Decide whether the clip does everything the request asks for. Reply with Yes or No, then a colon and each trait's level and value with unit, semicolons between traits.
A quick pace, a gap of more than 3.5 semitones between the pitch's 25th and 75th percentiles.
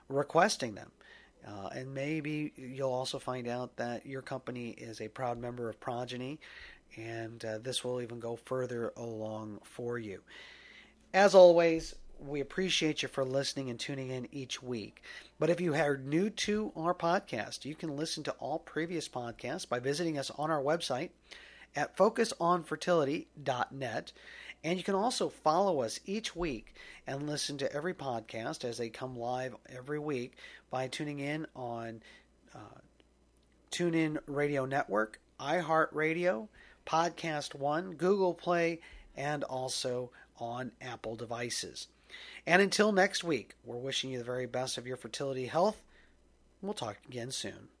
No: average, 150 wpm; average, 5.1 semitones